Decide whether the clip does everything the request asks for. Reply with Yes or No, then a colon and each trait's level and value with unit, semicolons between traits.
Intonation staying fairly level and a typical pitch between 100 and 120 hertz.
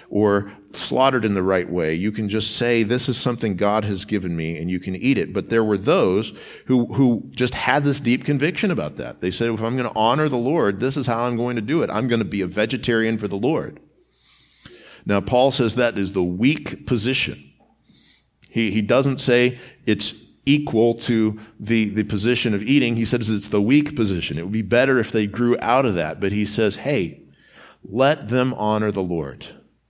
No: average, 3.3 semitones; low, 115 Hz